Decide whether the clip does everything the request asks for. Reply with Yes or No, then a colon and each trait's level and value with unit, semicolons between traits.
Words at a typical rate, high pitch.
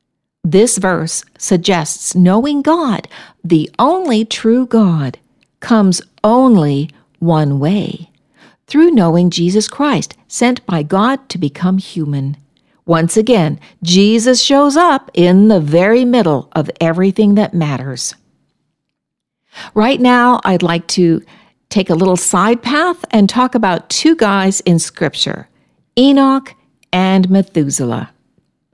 No: slow, 115 wpm; high, 195 Hz